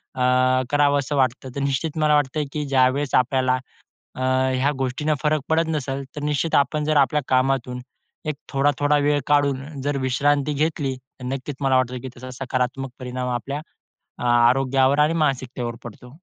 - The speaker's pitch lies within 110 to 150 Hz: Yes, low, 135 Hz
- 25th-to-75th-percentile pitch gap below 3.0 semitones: Yes, narrow, 2.4 semitones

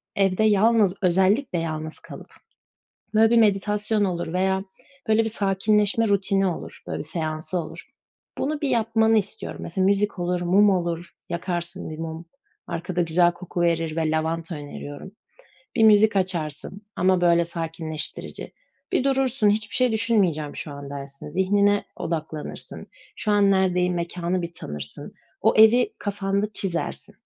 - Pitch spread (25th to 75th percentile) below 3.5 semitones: No, average, 3.8 semitones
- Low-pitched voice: No, medium, 185 Hz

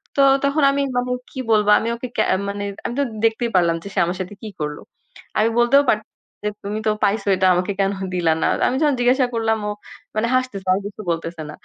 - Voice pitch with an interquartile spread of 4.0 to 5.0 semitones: Yes, average, 4.7 semitones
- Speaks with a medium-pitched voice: No, high, 215 Hz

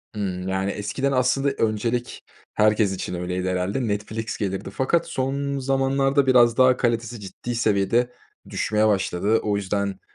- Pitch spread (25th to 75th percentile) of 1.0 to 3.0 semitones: No, average, 4.5 semitones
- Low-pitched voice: Yes, low, 110 Hz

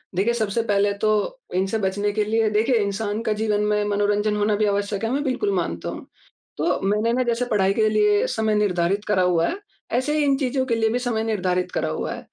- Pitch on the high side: Yes, high, 210 Hz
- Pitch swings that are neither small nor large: No, narrow, 2.1 semitones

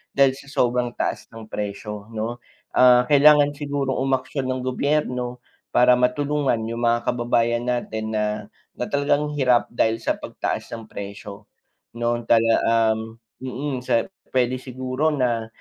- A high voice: No, low, 125 Hz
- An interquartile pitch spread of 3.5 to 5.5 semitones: No, average, 2.7 semitones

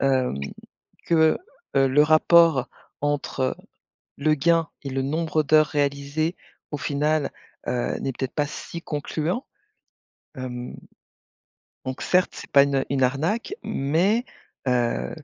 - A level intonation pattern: No, average, 3.0 semitones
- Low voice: No, medium, 145 Hz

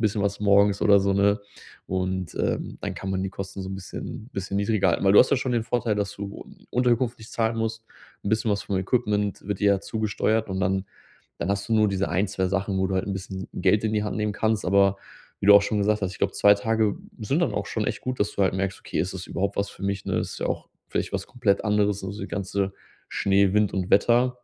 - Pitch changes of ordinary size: No, narrow, 1.8 semitones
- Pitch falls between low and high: No, low, 100 Hz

